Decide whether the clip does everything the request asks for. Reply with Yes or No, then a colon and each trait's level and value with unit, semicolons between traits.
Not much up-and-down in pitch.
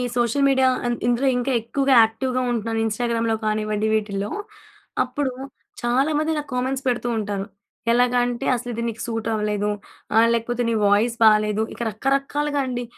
No: average, 3.1 semitones